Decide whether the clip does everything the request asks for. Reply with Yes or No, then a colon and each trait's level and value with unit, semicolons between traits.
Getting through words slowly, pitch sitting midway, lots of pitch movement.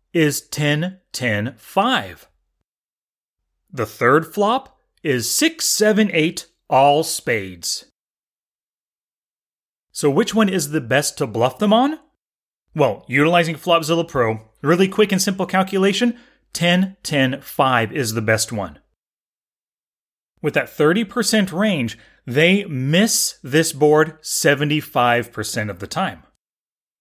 Yes: slow, 115 wpm; medium, 160 Hz; wide, 7.2 semitones